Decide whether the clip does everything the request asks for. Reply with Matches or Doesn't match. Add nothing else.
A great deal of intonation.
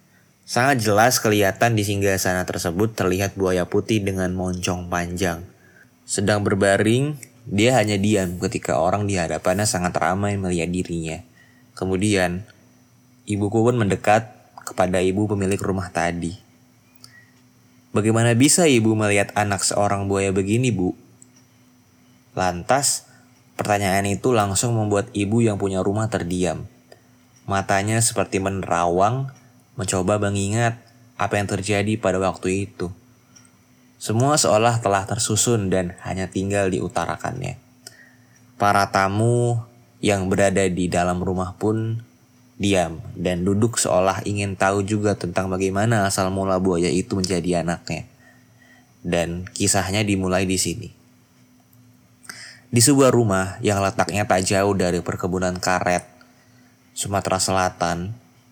Doesn't match